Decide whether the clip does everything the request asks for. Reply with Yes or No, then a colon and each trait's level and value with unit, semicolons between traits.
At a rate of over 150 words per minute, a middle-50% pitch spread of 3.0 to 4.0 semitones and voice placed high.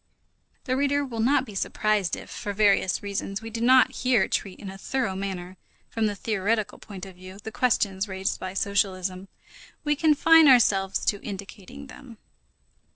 No: average, 165 wpm; average, 4.6 semitones; high, 205 Hz